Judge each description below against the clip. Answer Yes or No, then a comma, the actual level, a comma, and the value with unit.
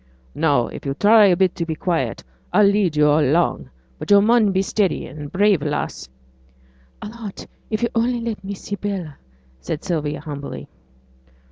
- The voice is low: No, medium, 180 Hz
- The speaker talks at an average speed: Yes, average, 180 wpm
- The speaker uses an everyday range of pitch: No, wide, 5.7 semitones